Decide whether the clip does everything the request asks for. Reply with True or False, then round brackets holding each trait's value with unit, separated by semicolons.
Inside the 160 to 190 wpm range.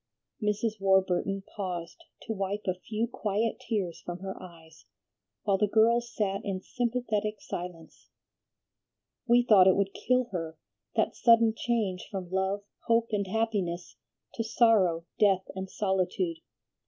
False (135 wpm)